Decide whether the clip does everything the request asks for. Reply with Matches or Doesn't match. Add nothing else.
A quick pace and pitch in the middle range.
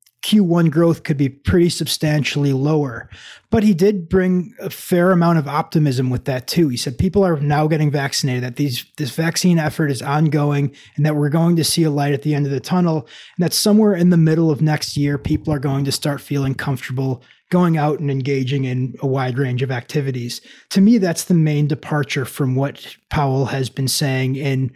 Matches